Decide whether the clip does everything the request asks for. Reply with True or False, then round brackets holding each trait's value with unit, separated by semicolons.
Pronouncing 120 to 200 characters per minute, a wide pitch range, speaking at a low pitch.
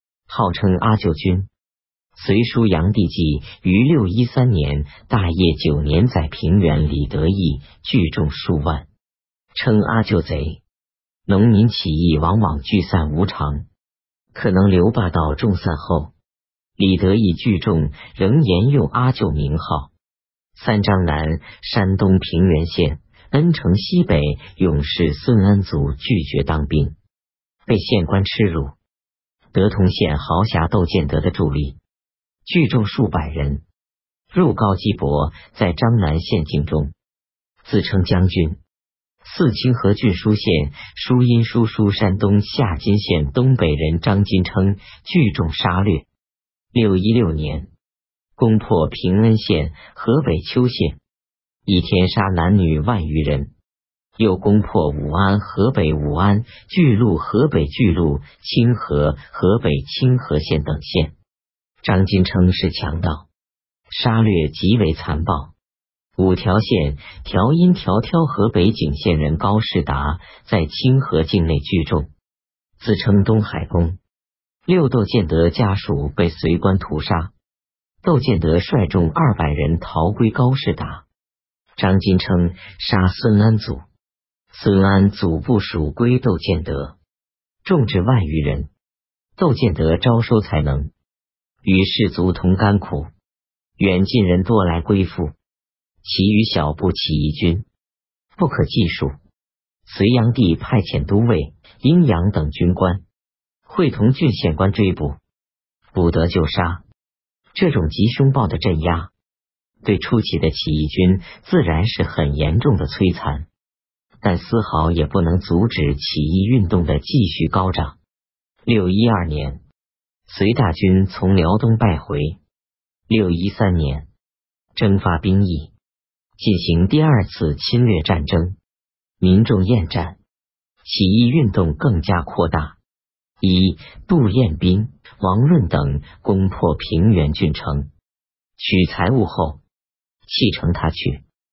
True (185 characters per minute; 5.8 semitones; 90 Hz)